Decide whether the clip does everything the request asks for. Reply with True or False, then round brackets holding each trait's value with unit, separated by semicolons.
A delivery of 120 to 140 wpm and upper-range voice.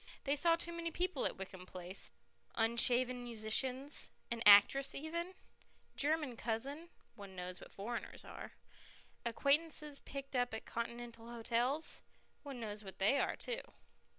True (135 wpm; 245 Hz)